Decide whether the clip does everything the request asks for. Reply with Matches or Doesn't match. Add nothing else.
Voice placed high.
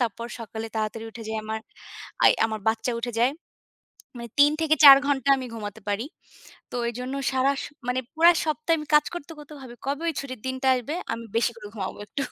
Matches